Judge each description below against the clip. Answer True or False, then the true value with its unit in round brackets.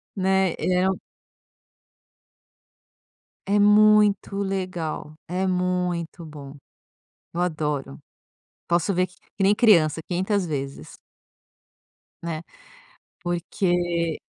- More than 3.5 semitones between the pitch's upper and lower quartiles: False (2.7 semitones)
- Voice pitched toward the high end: False (180 Hz)